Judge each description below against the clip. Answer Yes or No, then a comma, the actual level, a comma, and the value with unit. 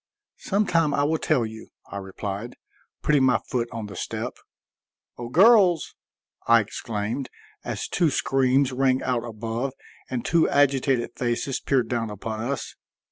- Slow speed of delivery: No, average, 145 wpm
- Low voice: Yes, low, 125 Hz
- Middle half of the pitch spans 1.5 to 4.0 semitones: Yes, average, 3.7 semitones